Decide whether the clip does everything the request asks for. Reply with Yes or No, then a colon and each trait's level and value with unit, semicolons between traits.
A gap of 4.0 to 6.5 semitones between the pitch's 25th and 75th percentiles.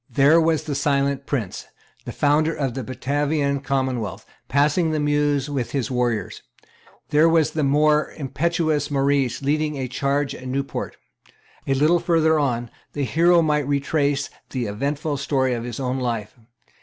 No: narrow, 2.4 semitones